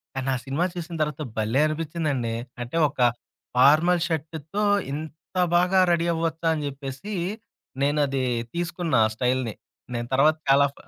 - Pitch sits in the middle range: Yes, medium, 150 Hz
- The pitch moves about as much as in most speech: Yes, average, 3.6 semitones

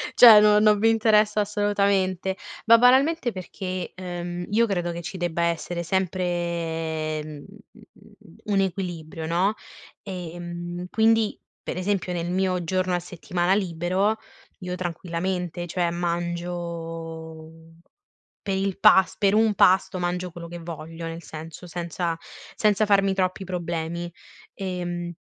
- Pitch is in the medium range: Yes, medium, 180 Hz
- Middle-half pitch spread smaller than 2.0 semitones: No, narrow, 2.4 semitones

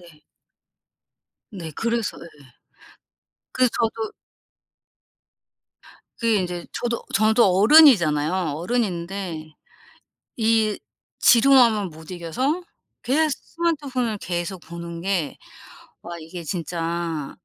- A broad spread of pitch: Yes, wide, 5.7 semitones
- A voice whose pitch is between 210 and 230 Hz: No, high, 190 Hz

